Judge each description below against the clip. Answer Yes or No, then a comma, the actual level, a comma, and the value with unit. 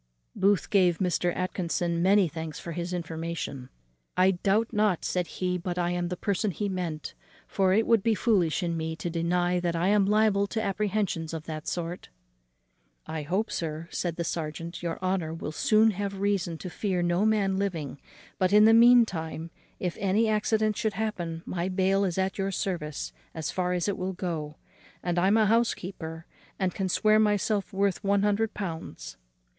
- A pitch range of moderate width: Yes, average, 3.2 semitones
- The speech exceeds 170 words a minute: Yes, average, 185 wpm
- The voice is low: No, medium, 185 Hz